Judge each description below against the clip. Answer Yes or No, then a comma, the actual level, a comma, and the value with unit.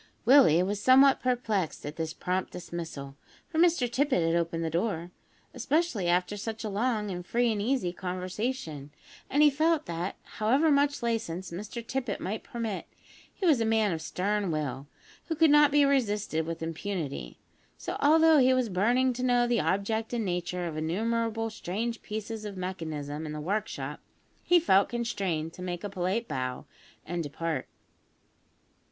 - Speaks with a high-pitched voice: Yes, high, 205 Hz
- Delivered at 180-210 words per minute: No, average, 165 wpm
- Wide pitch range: Yes, wide, 6.1 semitones